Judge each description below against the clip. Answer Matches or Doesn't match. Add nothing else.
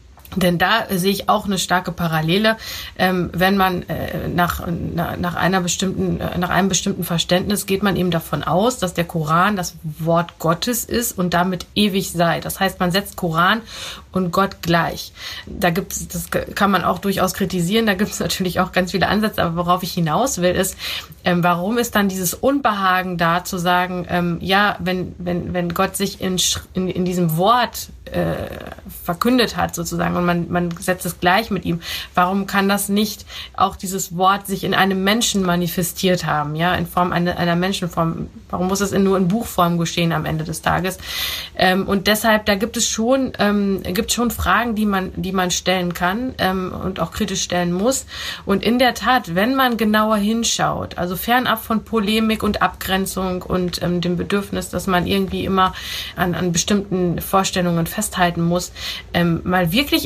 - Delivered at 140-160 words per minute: Doesn't match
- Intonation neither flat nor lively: Doesn't match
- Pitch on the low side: Doesn't match